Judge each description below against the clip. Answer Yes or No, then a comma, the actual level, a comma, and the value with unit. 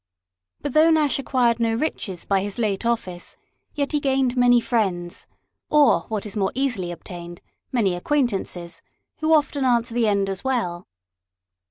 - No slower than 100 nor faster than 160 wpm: Yes, average, 155 wpm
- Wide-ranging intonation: Yes, wide, 5.7 semitones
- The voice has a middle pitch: No, high, 230 Hz